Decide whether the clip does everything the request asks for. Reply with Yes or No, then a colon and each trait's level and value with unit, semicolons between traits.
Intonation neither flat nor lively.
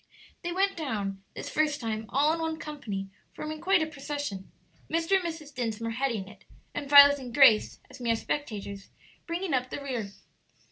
No: wide, 5.8 semitones